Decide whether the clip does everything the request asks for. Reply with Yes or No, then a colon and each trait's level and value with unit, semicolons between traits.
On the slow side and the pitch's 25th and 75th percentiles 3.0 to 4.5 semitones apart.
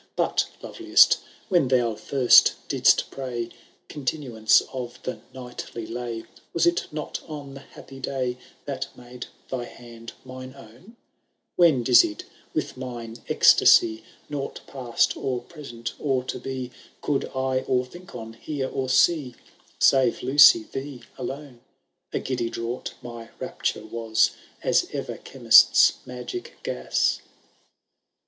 No: slow, 125 wpm; narrow, 2.5 semitones